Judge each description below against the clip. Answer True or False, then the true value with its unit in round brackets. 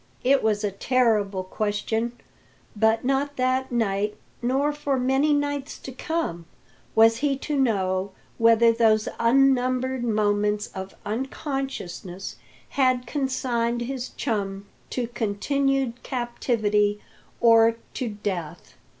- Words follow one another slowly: True (110 wpm)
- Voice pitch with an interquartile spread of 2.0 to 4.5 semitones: True (4.1 semitones)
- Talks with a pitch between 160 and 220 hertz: False (235 Hz)